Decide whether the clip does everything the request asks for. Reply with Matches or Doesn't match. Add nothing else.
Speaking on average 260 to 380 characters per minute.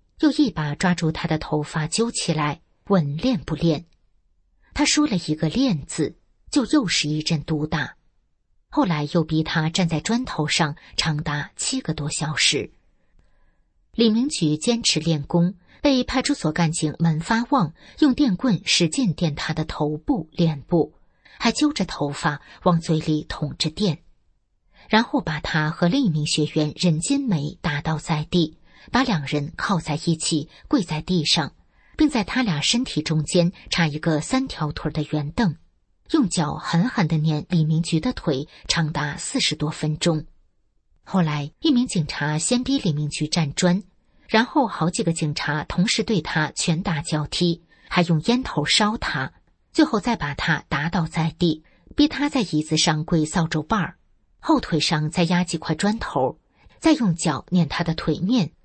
Doesn't match